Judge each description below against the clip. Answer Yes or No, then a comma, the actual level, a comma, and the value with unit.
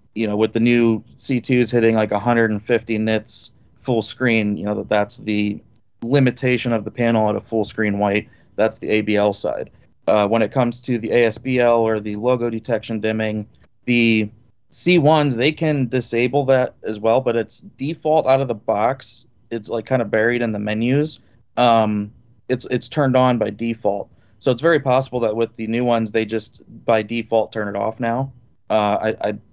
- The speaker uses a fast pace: No, average, 185 wpm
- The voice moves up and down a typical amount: No, narrow, 2.3 semitones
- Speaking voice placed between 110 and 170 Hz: Yes, low, 115 Hz